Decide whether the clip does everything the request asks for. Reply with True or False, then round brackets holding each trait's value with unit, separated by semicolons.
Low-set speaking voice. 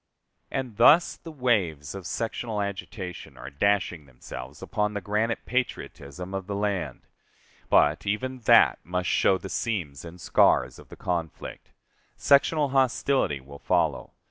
True (100 Hz)